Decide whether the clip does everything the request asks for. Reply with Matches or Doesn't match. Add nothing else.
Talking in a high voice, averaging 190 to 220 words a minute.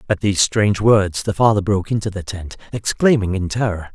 Doesn't match